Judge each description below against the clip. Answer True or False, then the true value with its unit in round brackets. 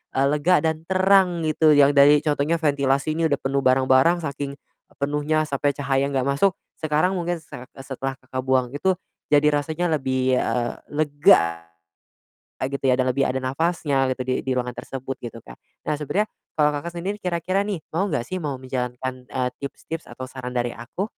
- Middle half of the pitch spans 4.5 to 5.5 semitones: False (3.6 semitones)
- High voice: False (140 Hz)